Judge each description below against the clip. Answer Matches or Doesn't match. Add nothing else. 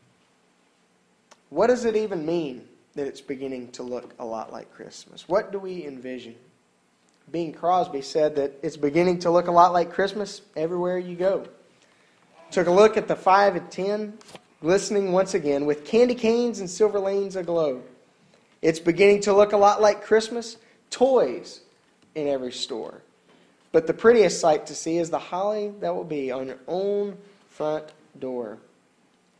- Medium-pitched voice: Matches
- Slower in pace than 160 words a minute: Doesn't match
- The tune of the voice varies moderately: Doesn't match